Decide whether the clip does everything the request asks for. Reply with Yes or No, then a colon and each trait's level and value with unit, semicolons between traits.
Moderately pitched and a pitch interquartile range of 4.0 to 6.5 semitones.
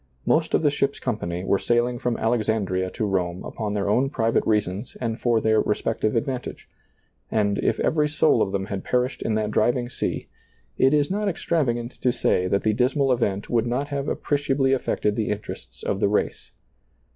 No: low, 115 Hz; average, 4.3 semitones